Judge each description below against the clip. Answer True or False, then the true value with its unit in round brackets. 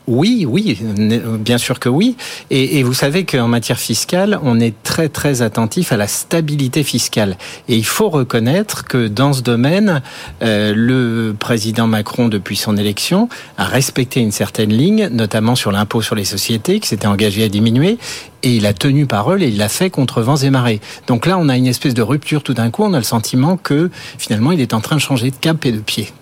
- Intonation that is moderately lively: True (4.4 semitones)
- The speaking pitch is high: False (125 Hz)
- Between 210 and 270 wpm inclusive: True (215 wpm)